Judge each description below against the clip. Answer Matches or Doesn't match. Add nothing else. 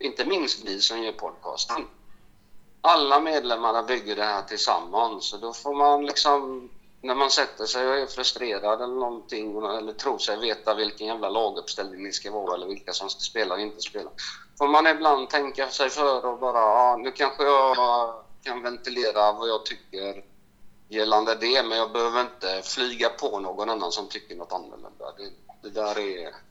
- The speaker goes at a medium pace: Matches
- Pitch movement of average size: Matches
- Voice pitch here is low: Matches